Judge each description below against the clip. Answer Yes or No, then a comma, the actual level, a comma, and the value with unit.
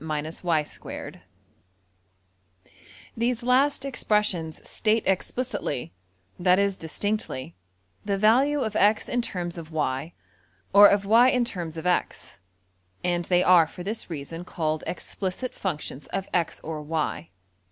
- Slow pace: Yes, slow, 110 wpm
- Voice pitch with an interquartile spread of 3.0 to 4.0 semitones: No, average, 5.2 semitones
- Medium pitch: Yes, medium, 180 Hz